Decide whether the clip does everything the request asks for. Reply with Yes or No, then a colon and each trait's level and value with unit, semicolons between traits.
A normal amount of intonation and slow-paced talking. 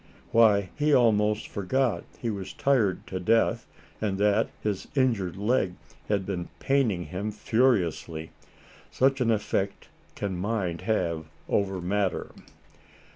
Yes: average, 3.7 semitones; slow, 125 wpm